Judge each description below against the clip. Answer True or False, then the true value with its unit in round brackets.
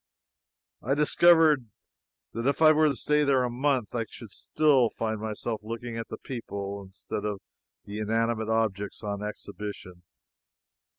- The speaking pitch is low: True (115 Hz)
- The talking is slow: False (150 wpm)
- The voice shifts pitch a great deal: False (4.6 semitones)